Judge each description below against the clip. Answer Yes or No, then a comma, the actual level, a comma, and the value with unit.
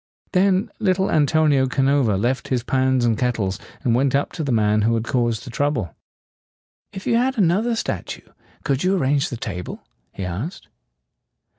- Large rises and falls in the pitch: Yes, wide, 6.2 semitones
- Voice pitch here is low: Yes, low, 130 Hz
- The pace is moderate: Yes, average, 175 wpm